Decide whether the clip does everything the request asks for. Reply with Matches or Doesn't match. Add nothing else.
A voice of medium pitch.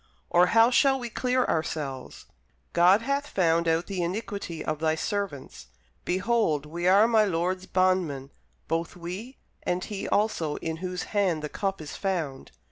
Matches